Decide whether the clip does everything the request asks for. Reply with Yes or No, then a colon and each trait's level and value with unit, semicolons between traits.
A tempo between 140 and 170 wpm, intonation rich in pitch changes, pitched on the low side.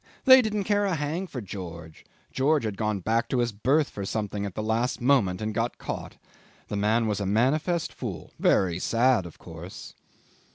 No: average, 190 wpm; wide, 5.9 semitones; low, 110 Hz